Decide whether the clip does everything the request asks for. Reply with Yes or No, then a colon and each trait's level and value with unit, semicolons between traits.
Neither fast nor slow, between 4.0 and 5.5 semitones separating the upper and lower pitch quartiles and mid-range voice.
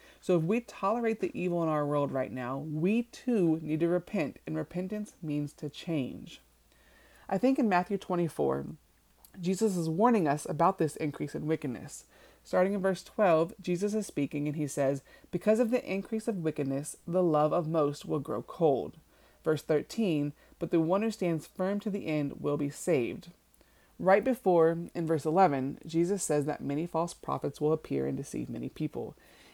Yes: average, 180 wpm; average, 4.6 semitones; medium, 165 Hz